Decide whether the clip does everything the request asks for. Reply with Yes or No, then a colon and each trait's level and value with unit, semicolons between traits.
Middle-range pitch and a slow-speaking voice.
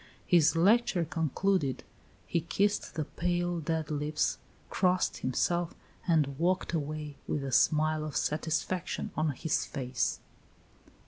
Yes: medium, 160 Hz; slow, 120 wpm